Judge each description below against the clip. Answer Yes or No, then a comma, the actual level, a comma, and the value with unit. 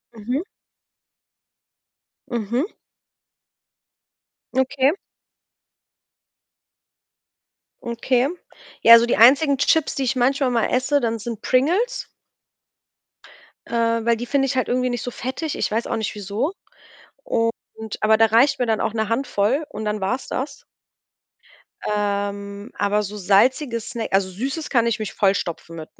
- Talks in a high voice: Yes, high, 235 Hz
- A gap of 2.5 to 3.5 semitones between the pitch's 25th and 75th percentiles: No, average, 3.9 semitones